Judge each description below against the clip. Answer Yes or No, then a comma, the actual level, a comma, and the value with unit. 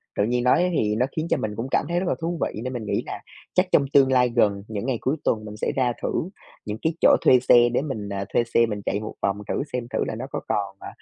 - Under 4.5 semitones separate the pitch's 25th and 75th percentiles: Yes, average, 3.9 semitones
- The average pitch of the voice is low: Yes, low, 120 Hz